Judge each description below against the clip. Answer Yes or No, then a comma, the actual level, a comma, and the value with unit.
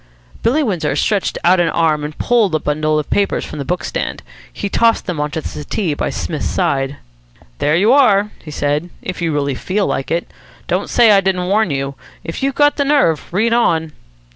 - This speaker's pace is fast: Yes, fast, 210 wpm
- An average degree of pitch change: No, wide, 5.7 semitones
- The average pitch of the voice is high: No, medium, 175 Hz